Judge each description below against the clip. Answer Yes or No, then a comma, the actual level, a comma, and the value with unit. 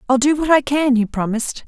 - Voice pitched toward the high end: Yes, very high, 265 Hz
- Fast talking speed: Yes, fast, 250 wpm